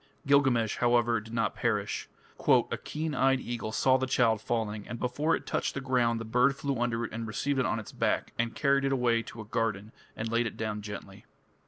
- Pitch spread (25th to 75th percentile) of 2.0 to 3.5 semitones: Yes, average, 2.9 semitones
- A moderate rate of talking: No, fast, 215 wpm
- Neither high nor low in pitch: No, low, 120 Hz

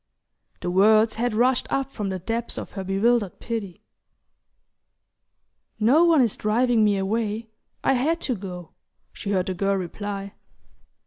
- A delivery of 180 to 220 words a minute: No, average, 145 wpm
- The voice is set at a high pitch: Yes, high, 215 Hz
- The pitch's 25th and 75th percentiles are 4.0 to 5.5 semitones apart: No, average, 3.5 semitones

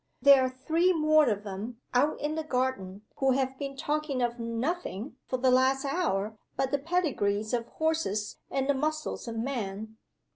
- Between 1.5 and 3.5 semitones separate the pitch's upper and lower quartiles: No, average, 4.9 semitones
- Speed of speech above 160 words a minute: Yes, average, 175 wpm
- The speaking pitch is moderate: No, very high, 260 Hz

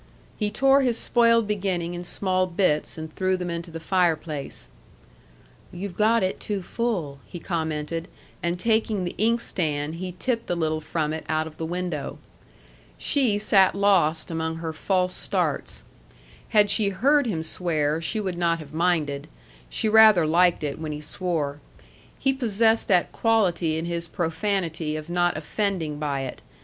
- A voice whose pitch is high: No, medium, 175 Hz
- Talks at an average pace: Yes, average, 160 wpm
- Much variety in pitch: No, average, 4.3 semitones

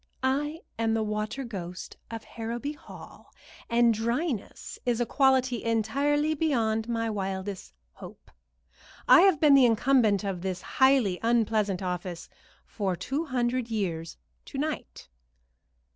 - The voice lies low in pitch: No, high, 230 Hz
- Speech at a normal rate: No, slow, 130 wpm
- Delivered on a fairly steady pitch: No, average, 4.5 semitones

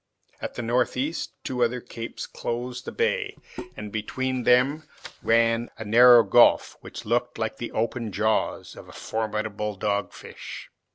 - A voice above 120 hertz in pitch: No, low, 115 Hz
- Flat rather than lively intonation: Yes, narrow, 2.3 semitones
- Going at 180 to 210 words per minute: No, average, 155 wpm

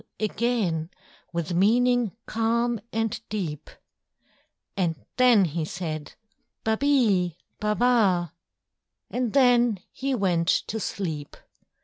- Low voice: No, high, 210 Hz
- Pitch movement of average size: No, wide, 5.7 semitones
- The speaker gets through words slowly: Yes, slow, 105 wpm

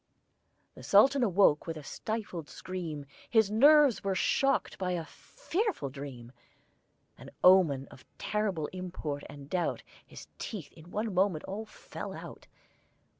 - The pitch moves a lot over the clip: Yes, wide, 5.8 semitones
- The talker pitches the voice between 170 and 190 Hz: Yes, medium, 185 Hz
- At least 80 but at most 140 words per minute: Yes, slow, 135 wpm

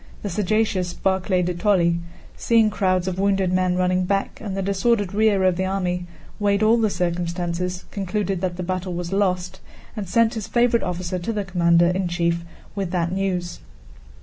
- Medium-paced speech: Yes, average, 175 wpm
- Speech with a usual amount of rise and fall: No, narrow, 2.1 semitones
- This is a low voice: No, medium, 185 Hz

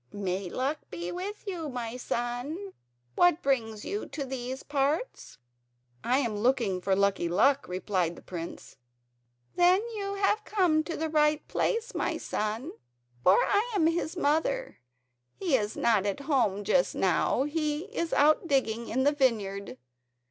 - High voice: Yes, very high, 275 Hz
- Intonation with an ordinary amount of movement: No, wide, 7.8 semitones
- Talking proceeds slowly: No, average, 150 wpm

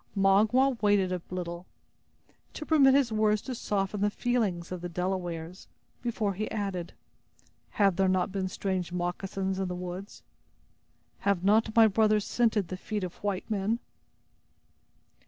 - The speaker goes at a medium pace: Yes, average, 145 wpm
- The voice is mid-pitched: No, high, 195 Hz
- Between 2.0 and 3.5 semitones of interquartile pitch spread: Yes, average, 2.8 semitones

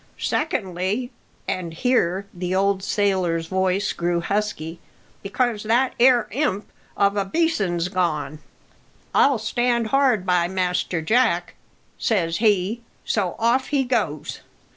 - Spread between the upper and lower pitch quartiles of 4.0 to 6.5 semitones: Yes, average, 4.9 semitones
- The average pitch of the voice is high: Yes, high, 200 Hz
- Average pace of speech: No, slow, 120 wpm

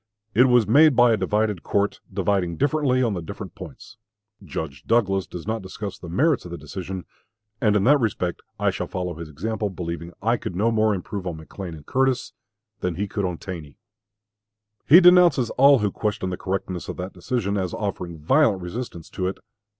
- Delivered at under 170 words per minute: No, average, 190 wpm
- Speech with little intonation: No, average, 4.7 semitones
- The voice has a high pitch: No, low, 100 Hz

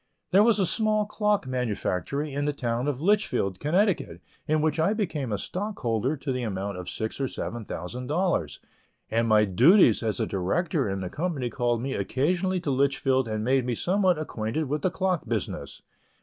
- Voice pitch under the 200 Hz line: Yes, low, 135 Hz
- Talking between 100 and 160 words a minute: No, average, 185 wpm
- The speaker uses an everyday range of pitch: No, wide, 7.5 semitones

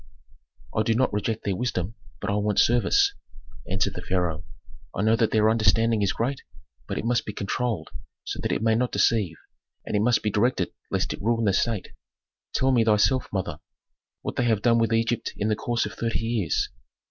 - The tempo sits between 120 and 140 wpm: No, average, 200 wpm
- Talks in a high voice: No, low, 110 Hz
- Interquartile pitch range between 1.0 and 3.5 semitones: Yes, narrow, 2.5 semitones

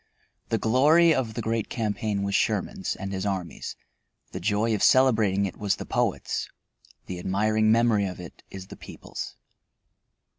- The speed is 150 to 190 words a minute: Yes, average, 155 wpm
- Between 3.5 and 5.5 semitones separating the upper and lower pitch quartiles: No, average, 2.7 semitones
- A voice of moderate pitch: No, low, 105 Hz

